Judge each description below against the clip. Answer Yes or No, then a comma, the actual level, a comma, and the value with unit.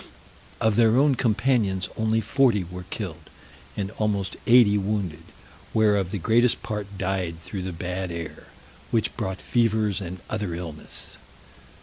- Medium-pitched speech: No, low, 100 Hz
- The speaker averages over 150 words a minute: No, slow, 135 wpm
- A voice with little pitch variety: No, average, 3.4 semitones